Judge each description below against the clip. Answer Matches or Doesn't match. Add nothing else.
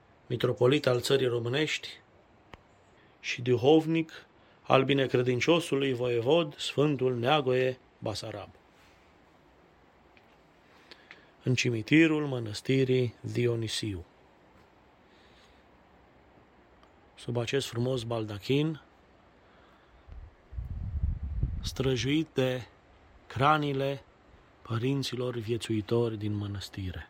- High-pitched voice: Doesn't match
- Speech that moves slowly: Matches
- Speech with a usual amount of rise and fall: Matches